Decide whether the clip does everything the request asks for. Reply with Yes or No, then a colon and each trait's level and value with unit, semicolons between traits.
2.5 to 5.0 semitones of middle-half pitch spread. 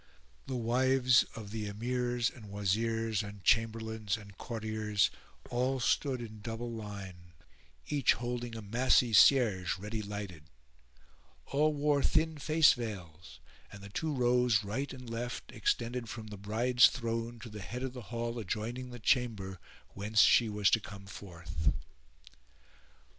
Yes: average, 3.2 semitones